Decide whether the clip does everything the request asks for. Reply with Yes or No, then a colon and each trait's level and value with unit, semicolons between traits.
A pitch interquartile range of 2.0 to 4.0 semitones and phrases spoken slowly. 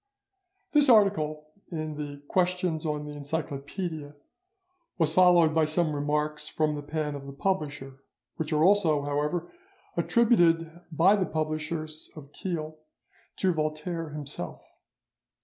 Yes: narrow, 2.6 semitones; slow, 125 wpm